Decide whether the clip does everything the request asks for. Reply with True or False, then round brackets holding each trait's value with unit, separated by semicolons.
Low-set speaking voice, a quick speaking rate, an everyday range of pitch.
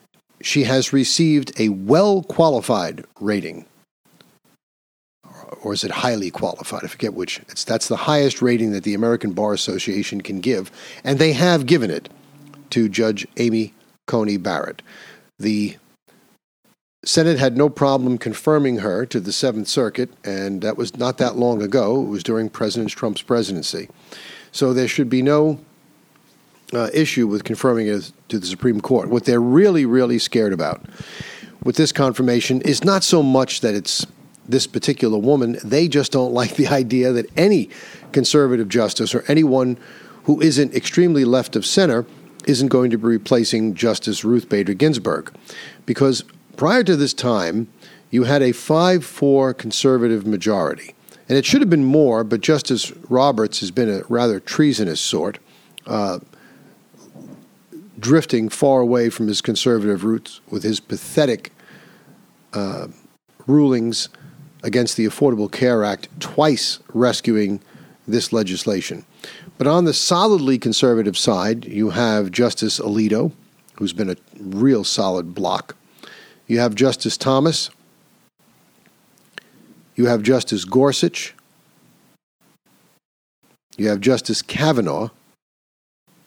False (125 Hz; 135 wpm; 4.4 semitones)